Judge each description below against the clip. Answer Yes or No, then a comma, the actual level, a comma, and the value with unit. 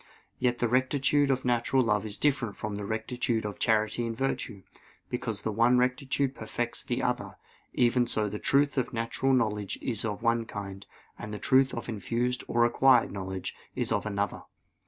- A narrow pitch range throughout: No, average, 3.1 semitones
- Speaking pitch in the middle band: No, low, 115 Hz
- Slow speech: No, average, 180 wpm